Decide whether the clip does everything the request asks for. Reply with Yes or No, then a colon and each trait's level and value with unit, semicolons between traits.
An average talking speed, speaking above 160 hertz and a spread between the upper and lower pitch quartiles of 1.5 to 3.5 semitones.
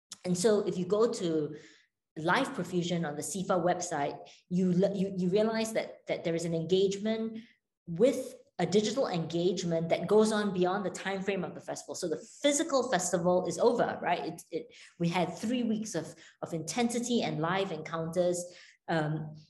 No: average, 170 wpm; medium, 185 Hz; average, 4.3 semitones